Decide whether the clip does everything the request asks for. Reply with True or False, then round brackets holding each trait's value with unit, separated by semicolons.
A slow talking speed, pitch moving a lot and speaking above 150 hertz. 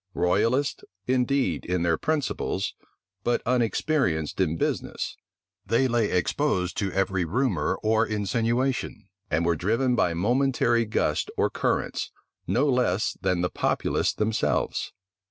False (120 wpm; 5.8 semitones; 110 Hz)